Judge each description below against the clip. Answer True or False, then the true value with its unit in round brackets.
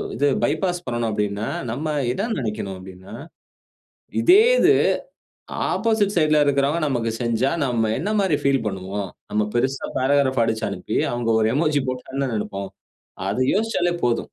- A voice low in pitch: True (130 Hz)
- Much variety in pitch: True (5.7 semitones)